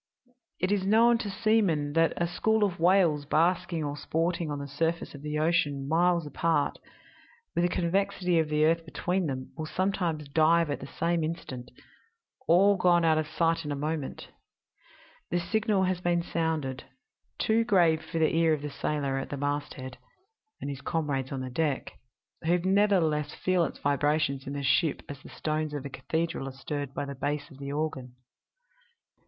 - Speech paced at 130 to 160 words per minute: No, average, 180 wpm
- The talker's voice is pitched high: No, medium, 160 Hz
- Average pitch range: Yes, average, 3.4 semitones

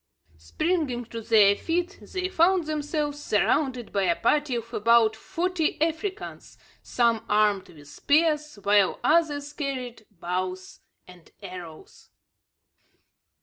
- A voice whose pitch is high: Yes, high, 245 Hz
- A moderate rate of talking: No, slow, 110 wpm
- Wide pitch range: Yes, wide, 7.3 semitones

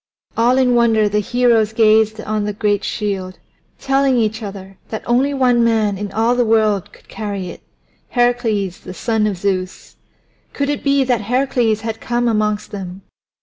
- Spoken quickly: No, average, 170 wpm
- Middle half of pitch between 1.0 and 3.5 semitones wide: Yes, average, 2.8 semitones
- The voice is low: No, high, 220 Hz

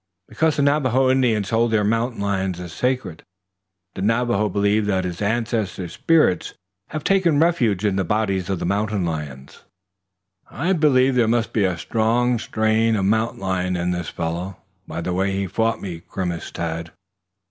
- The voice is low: Yes, low, 105 Hz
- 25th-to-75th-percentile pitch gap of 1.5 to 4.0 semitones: No, average, 4.5 semitones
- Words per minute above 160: Yes, average, 170 wpm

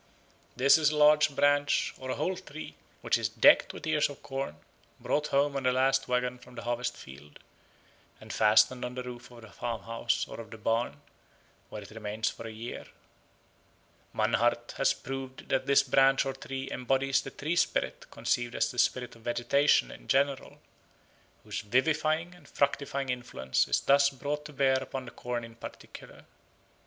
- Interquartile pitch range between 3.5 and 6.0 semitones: No, average, 2.8 semitones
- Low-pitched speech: Yes, low, 130 Hz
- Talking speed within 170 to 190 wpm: Yes, average, 175 wpm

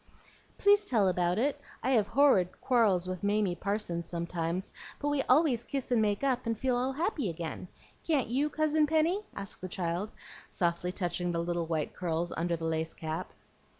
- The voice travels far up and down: Yes, wide, 7.5 semitones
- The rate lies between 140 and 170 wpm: No, average, 180 wpm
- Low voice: No, high, 200 Hz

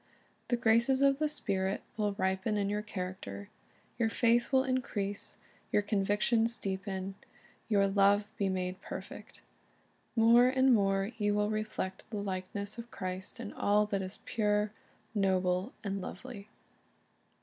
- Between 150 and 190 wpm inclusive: No, average, 140 wpm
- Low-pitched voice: No, high, 205 Hz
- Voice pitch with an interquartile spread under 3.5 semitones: Yes, average, 2.8 semitones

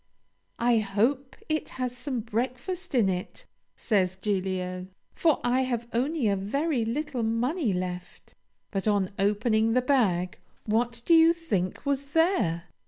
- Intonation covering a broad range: Yes, wide, 5.9 semitones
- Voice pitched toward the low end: No, high, 230 Hz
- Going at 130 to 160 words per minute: Yes, average, 140 wpm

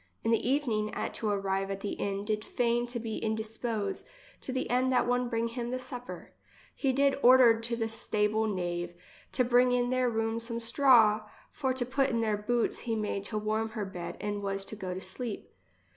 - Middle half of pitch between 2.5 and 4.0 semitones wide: Yes, average, 2.8 semitones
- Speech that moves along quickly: Yes, fast, 215 wpm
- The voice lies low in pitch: No, high, 225 Hz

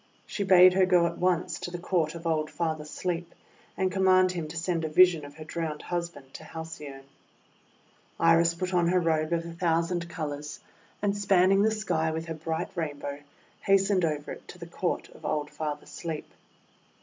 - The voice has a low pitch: No, medium, 170 Hz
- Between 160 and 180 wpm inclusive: No, average, 195 wpm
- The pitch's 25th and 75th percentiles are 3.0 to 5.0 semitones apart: No, narrow, 2.5 semitones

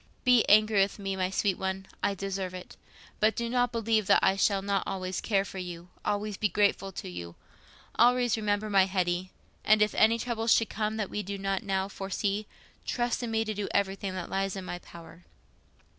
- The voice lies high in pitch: Yes, high, 200 Hz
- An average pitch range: No, narrow, 2.1 semitones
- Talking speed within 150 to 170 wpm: No, average, 195 wpm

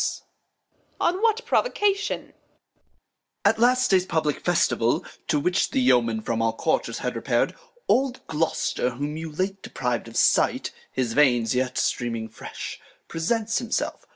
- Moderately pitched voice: Yes, medium, 155 Hz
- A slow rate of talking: No, average, 145 wpm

